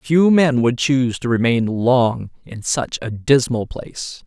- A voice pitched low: Yes, low, 125 Hz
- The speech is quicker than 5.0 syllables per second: No, 3.9 syllables/s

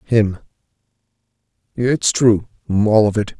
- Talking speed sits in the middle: No, slow, 105 wpm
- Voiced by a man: Yes, male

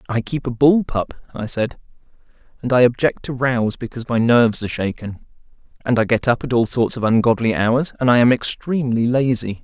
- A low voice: Yes, low, 120 Hz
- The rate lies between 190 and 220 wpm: Yes, average, 200 wpm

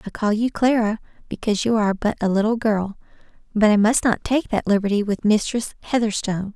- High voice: Yes, high, 215 Hz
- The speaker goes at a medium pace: Yes, average, 190 wpm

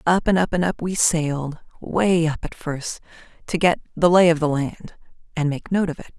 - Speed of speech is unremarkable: No, fast, 225 wpm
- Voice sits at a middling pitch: Yes, medium, 165 Hz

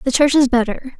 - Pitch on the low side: No, very high, 260 Hz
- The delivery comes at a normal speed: No, fast, 240 wpm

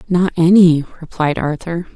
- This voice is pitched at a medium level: Yes, medium, 170 Hz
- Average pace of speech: No, slow, 125 wpm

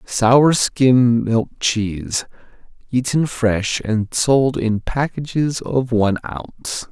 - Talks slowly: Yes, slow, 115 wpm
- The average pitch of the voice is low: Yes, low, 120 Hz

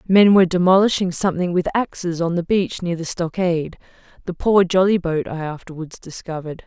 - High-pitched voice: No, medium, 175 Hz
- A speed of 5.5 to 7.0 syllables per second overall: Yes, 5.7 syllables/s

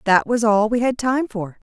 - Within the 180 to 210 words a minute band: No, fast, 240 wpm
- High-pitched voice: Yes, high, 225 Hz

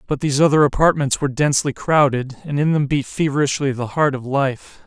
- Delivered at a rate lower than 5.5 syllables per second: No, 5.9 syllables/s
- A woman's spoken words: No, male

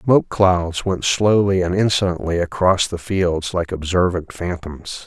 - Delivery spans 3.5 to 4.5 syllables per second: Yes, 4.2 syllables/s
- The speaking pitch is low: Yes, very low, 90 Hz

